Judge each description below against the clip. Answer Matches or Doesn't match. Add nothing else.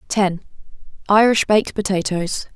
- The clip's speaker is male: Doesn't match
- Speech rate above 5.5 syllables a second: Doesn't match